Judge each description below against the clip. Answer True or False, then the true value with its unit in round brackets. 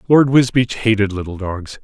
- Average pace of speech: True (165 wpm)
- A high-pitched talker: False (110 Hz)